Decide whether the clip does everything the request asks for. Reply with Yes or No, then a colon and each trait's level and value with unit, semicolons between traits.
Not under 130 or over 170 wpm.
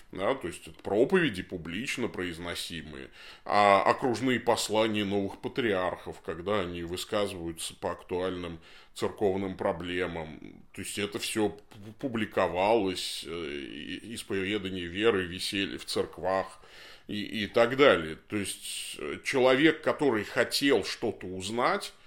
No: slow, 110 wpm